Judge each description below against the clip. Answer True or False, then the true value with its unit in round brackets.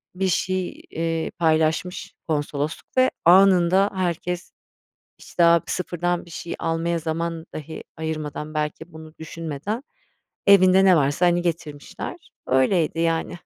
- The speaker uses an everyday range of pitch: False (2.2 semitones)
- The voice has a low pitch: False (165 Hz)